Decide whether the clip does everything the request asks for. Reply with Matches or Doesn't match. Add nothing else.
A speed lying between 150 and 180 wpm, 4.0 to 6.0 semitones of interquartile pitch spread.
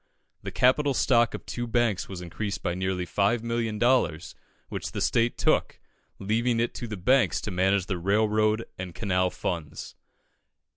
Matches